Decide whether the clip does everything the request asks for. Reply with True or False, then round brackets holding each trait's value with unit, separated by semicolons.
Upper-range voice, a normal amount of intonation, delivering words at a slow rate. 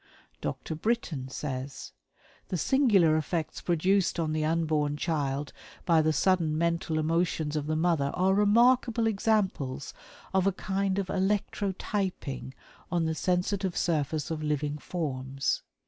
False (165 Hz; 4.1 semitones; 130 wpm)